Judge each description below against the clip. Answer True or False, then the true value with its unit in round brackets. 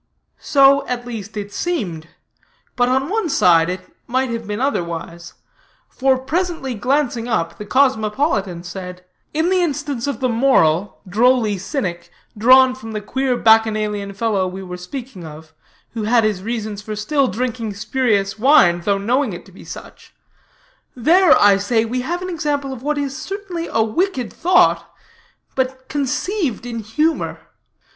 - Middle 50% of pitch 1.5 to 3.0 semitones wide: False (5.3 semitones)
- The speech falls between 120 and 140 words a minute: False (155 wpm)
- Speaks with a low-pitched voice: False (235 Hz)